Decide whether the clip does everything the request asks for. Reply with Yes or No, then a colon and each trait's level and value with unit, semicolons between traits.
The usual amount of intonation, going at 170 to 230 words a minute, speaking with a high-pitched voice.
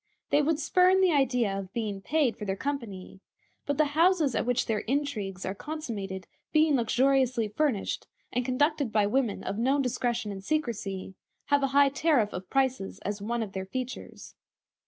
No: wide, 5.8 semitones; average, 175 wpm; high, 245 Hz